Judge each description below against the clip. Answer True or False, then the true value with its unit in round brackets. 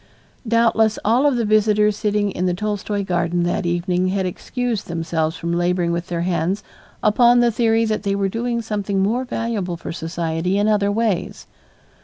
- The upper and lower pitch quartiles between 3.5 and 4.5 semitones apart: True (4.1 semitones)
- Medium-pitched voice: False (200 Hz)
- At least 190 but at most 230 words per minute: False (175 wpm)